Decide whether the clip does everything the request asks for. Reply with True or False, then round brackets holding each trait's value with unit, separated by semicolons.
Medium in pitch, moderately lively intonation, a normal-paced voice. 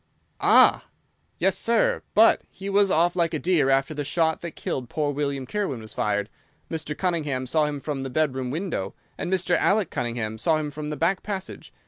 True (155 Hz; 4.8 semitones; 190 wpm)